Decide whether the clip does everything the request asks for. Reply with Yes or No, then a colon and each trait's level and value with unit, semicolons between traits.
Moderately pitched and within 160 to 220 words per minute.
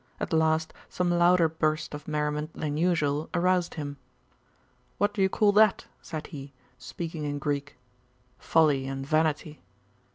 No: medium, 155 Hz; average, 140 wpm